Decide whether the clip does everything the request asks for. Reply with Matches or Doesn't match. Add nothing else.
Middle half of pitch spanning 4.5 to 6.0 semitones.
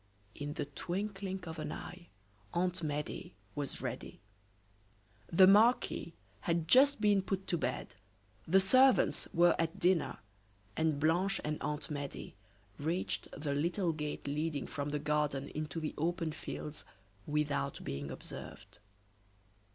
Doesn't match